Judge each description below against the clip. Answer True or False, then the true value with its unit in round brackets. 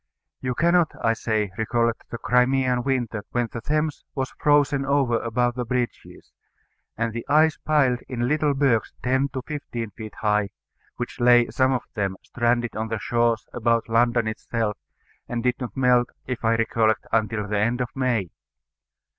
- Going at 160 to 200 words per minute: True (165 wpm)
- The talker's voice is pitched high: False (120 Hz)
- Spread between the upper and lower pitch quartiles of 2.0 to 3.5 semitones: True (2.4 semitones)